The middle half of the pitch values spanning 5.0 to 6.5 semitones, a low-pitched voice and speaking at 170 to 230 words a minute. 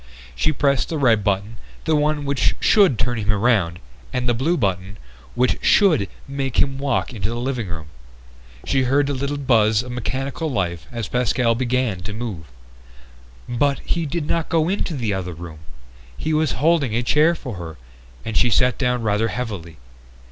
Yes: average, 5.3 semitones; low, 125 Hz; average, 175 wpm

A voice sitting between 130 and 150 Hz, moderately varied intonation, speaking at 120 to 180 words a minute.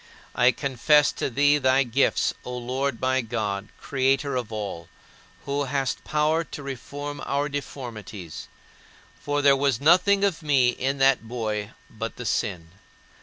Yes: low, 135 Hz; average, 3.2 semitones; average, 145 wpm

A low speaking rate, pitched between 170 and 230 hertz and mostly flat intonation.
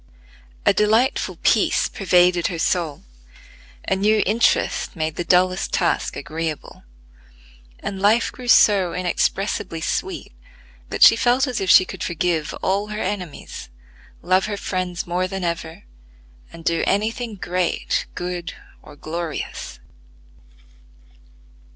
No: slow, 125 wpm; medium, 185 Hz; average, 3.3 semitones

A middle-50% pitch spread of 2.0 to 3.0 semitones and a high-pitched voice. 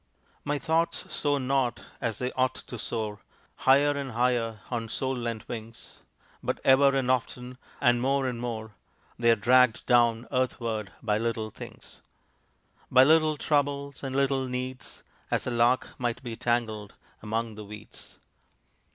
No: narrow, 2.6 semitones; low, 125 Hz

